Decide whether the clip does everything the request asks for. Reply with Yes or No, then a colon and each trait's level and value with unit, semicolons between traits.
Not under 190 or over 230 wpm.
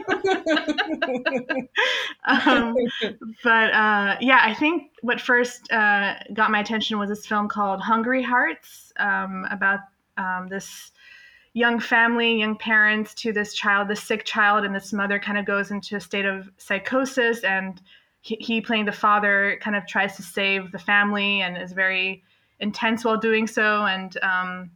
No: average, 155 wpm